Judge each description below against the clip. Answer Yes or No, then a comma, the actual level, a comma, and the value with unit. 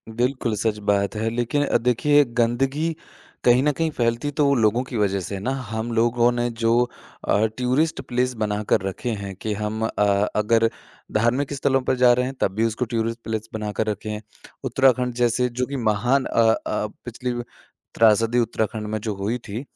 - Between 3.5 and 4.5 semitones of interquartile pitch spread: No, narrow, 2.6 semitones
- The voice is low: Yes, low, 115 Hz